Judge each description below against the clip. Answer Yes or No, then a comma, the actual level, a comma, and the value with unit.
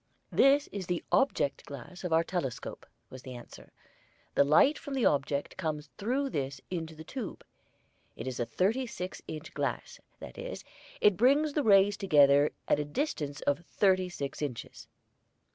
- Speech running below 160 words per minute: No, average, 165 wpm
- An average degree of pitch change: No, wide, 8.1 semitones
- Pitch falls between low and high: Yes, medium, 175 Hz